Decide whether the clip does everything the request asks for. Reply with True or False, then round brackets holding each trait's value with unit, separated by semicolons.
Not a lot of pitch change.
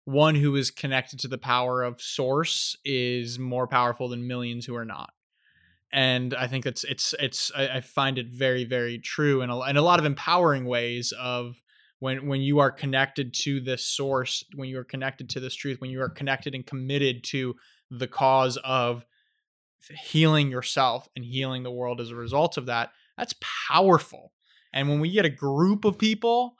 True (2.1 semitones)